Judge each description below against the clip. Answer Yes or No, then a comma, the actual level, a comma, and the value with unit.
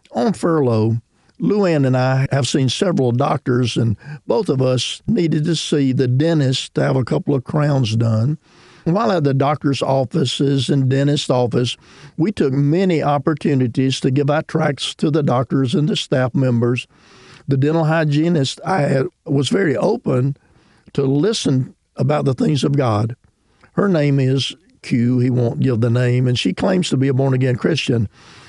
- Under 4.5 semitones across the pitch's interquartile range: Yes, average, 2.9 semitones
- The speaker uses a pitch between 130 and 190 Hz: Yes, medium, 140 Hz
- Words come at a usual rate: Yes, average, 170 wpm